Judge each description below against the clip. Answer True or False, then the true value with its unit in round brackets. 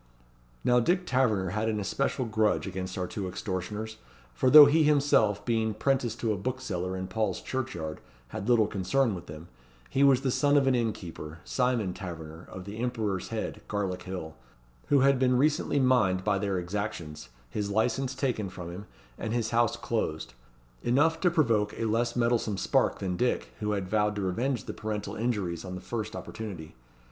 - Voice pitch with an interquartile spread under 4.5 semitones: False (5.1 semitones)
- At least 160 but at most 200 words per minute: True (180 wpm)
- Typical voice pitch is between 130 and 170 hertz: False (110 Hz)